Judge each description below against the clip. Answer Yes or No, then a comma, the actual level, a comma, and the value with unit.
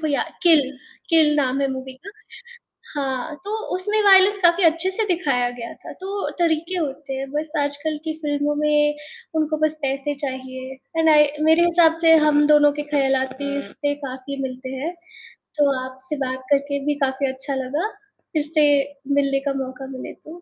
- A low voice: No, very high, 290 Hz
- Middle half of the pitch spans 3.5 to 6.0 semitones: No, average, 3.1 semitones